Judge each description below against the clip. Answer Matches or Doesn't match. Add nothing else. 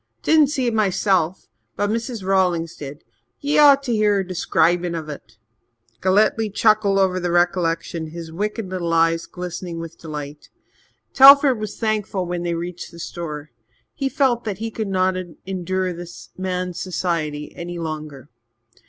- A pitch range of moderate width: Matches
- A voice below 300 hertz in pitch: Matches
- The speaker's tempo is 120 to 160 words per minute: Matches